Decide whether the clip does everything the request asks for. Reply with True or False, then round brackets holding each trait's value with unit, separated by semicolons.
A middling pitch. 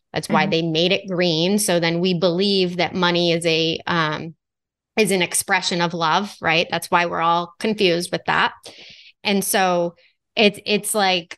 True (175 Hz)